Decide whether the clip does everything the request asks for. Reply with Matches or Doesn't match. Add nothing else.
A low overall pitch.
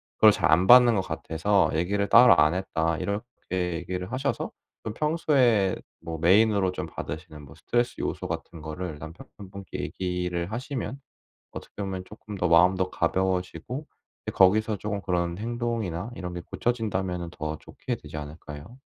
Matches